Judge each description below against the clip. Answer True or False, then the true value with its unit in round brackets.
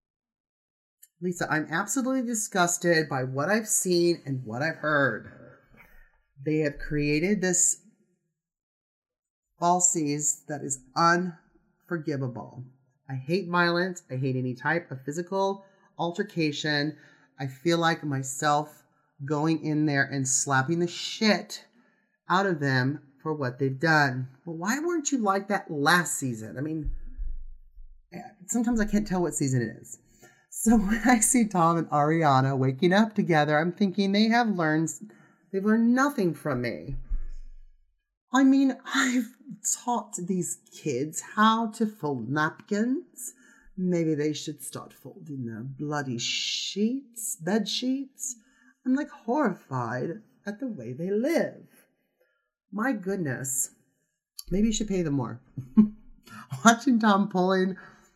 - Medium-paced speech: False (130 wpm)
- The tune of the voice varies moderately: False (6.4 semitones)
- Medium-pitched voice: True (170 Hz)